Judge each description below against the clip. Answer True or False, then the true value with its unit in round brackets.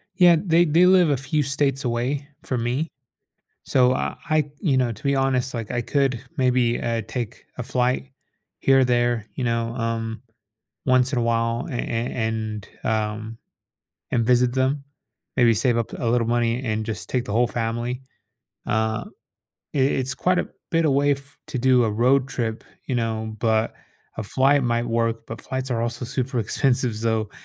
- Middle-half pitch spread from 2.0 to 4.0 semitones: True (2.7 semitones)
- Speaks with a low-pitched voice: True (120 Hz)